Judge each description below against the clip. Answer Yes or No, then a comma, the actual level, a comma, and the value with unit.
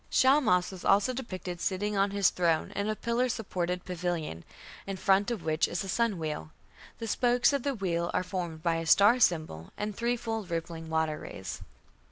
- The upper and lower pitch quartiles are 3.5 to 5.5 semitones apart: Yes, average, 4.9 semitones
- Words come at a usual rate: Yes, average, 185 wpm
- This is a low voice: No, high, 190 Hz